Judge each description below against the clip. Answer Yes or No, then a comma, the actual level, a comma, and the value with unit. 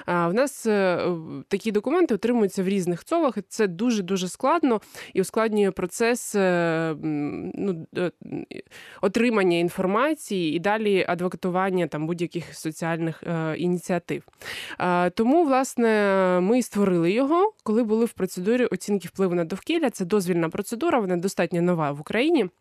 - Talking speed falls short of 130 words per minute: Yes, average, 120 wpm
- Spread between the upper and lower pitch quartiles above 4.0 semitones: Yes, average, 4.5 semitones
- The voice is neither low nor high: No, high, 195 Hz